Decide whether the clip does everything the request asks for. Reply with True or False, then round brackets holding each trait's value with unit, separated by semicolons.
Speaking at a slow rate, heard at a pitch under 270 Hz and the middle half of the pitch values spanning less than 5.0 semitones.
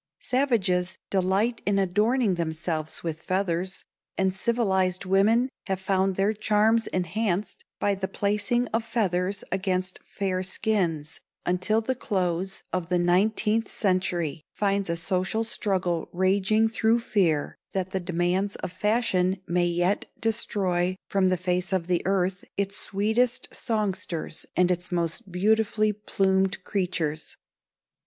True (130 wpm; 190 Hz; 2.8 semitones)